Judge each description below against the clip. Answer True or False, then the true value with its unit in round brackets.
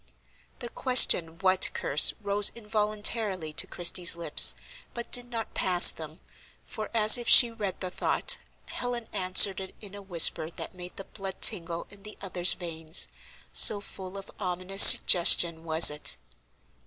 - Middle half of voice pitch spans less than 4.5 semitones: True (3.7 semitones)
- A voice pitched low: False (190 Hz)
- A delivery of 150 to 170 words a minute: True (155 wpm)